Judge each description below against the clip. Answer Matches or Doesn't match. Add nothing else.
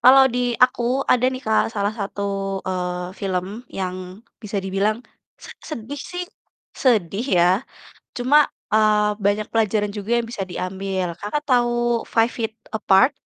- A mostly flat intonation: Doesn't match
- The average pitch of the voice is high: Matches